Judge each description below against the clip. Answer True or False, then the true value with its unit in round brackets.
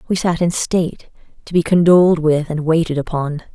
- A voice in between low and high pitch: True (165 Hz)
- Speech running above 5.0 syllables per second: True (5.4 syllables/s)